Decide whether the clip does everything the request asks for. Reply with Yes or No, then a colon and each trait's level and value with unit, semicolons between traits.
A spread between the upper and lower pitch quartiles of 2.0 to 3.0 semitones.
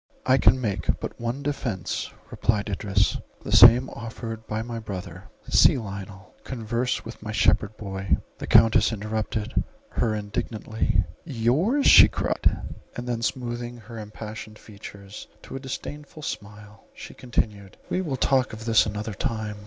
Yes: narrow, 2.6 semitones